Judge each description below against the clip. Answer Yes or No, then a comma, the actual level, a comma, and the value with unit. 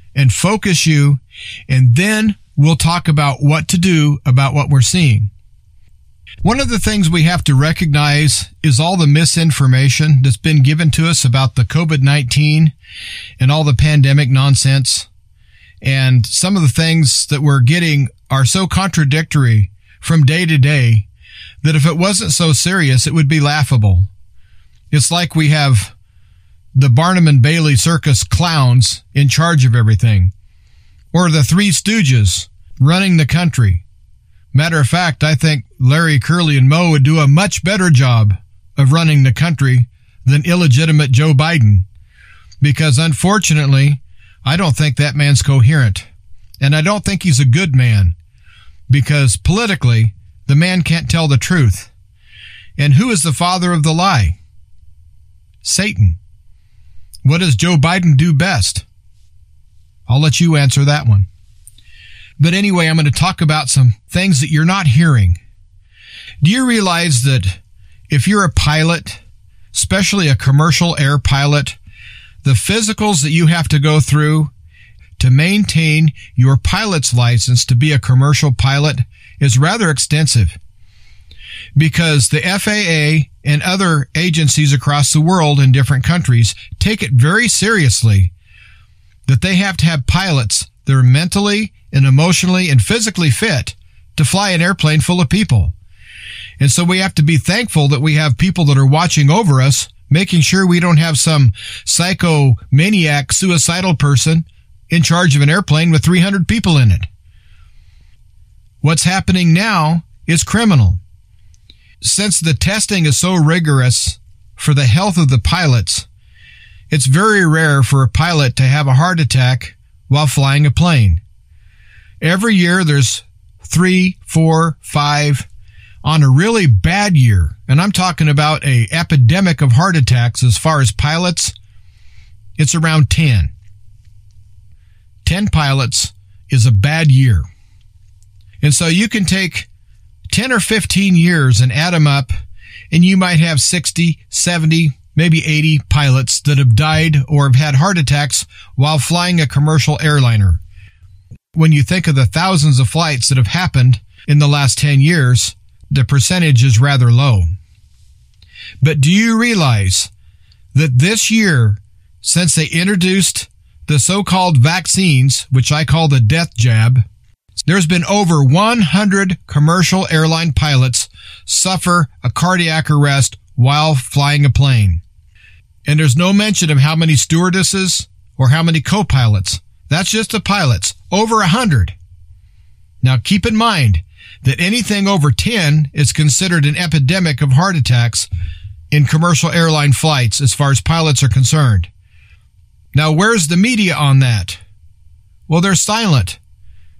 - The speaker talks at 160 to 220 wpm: No, average, 145 wpm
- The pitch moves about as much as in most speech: No, wide, 7.8 semitones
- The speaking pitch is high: No, medium, 140 Hz